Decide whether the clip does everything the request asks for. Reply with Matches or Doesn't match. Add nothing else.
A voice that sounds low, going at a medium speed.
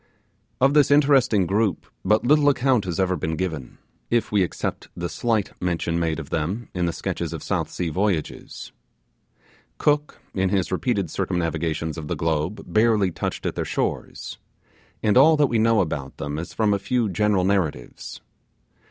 Matches